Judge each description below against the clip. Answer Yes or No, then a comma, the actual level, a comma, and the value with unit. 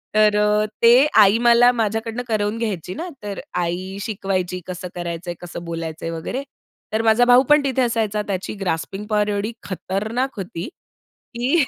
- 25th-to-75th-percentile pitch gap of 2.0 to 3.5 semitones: No, average, 4.0 semitones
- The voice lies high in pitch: Yes, high, 210 Hz